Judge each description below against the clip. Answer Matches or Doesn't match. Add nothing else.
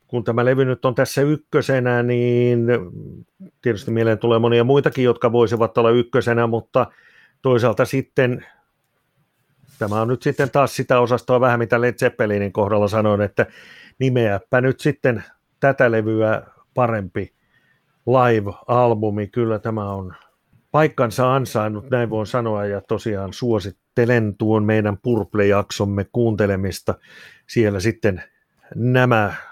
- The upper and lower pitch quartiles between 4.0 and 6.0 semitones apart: Doesn't match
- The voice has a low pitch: Matches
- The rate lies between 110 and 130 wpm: Matches